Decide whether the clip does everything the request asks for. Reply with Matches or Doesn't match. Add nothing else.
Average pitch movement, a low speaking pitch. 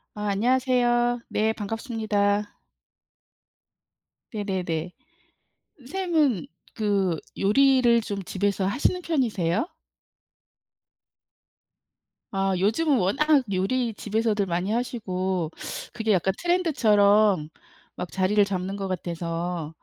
Doesn't match